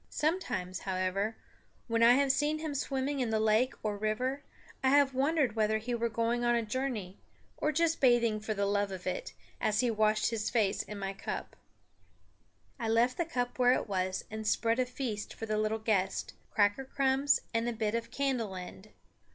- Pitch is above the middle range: Yes, high, 230 Hz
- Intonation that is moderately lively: Yes, average, 3.7 semitones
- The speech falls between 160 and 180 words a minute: No, average, 190 wpm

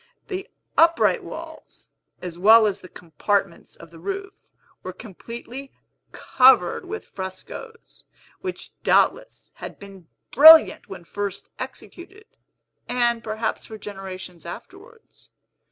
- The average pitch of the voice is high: Yes, high, 220 Hz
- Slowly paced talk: Yes, slow, 110 wpm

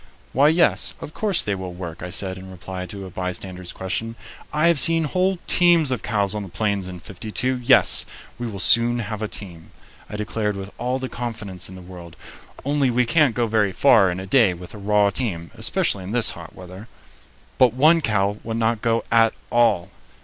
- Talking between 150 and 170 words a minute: No, fast, 205 wpm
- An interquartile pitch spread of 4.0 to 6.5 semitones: Yes, average, 4.6 semitones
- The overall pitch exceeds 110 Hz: No, low, 105 Hz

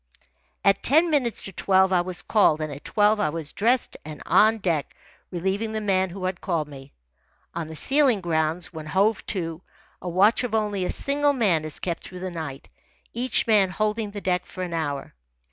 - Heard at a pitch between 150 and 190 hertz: Yes, medium, 185 Hz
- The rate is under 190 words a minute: No, average, 195 wpm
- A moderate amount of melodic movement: Yes, average, 4.5 semitones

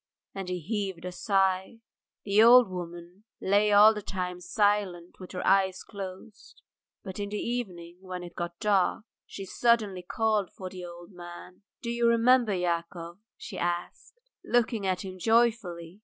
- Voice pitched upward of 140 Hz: Yes, high, 190 Hz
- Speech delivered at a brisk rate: No, average, 155 wpm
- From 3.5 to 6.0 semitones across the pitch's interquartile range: No, average, 3.0 semitones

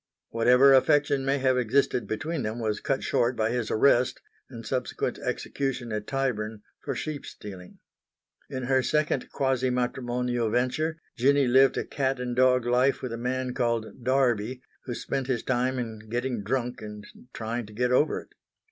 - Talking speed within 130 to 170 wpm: Yes, average, 165 wpm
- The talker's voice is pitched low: Yes, low, 125 Hz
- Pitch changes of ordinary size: No, narrow, 2.3 semitones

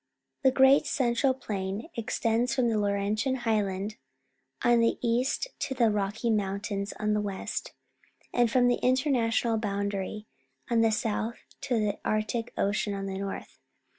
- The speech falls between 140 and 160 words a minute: Yes, average, 145 wpm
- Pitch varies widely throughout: No, average, 3.0 semitones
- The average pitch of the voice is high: Yes, high, 225 Hz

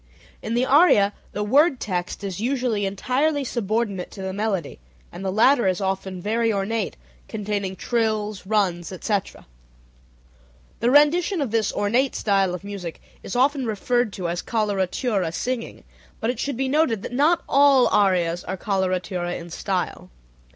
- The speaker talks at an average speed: Yes, average, 150 wpm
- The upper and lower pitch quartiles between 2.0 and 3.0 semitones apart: No, average, 4.6 semitones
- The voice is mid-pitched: No, high, 210 Hz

